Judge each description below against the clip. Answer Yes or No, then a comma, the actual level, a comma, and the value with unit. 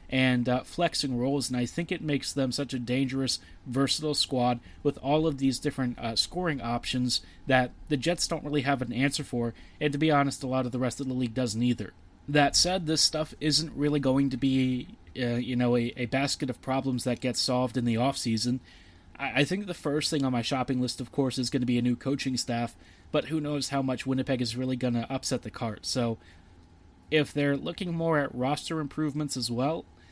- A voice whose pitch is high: No, low, 130 Hz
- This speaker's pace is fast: Yes, fast, 225 wpm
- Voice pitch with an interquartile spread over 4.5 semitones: No, average, 2.9 semitones